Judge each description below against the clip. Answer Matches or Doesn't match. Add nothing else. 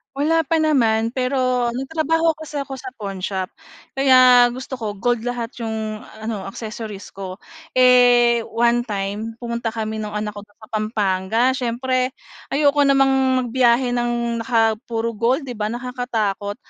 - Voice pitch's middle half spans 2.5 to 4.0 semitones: Matches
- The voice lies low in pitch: Doesn't match